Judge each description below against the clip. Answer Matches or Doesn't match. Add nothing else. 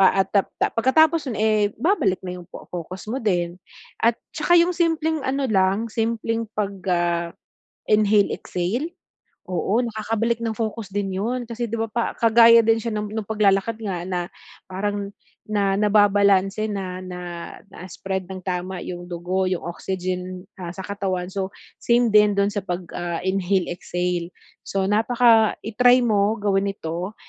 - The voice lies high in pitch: Matches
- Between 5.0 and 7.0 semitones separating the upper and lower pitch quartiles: Doesn't match